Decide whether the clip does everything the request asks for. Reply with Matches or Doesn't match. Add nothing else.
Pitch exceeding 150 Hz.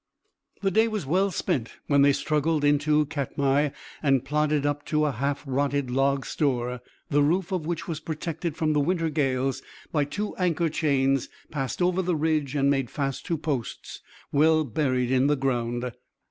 Doesn't match